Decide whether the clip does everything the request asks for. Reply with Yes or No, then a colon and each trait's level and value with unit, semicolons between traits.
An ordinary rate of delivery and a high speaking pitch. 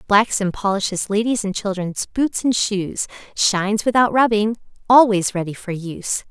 Yes: average, 150 wpm; high, 205 Hz